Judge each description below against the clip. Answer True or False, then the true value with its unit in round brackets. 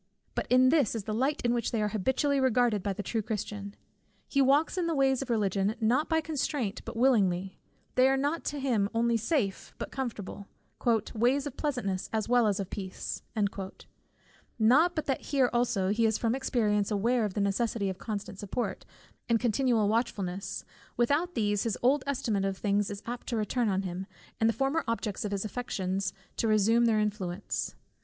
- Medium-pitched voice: False (225 Hz)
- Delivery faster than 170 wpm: True (185 wpm)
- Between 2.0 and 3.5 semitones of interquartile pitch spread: False (4.2 semitones)